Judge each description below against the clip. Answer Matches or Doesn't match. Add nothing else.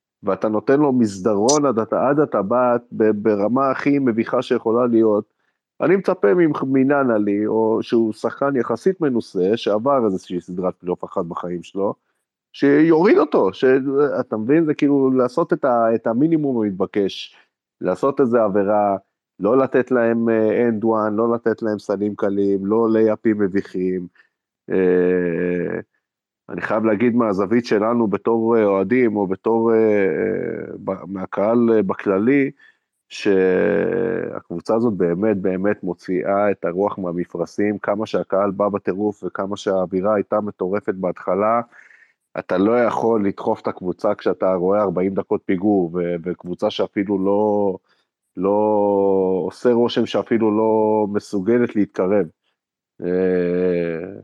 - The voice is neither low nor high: Doesn't match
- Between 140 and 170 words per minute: Doesn't match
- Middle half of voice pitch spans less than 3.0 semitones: Doesn't match